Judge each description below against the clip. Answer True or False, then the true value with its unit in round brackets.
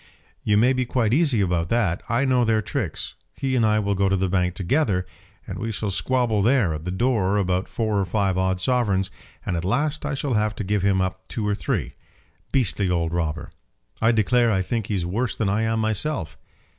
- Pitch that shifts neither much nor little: True (4.2 semitones)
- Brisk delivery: True (215 wpm)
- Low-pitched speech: True (105 Hz)